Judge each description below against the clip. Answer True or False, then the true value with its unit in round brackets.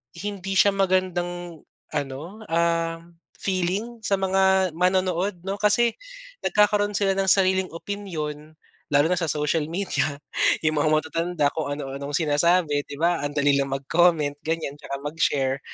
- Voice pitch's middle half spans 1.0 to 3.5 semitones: False (4.4 semitones)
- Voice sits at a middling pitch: True (170 Hz)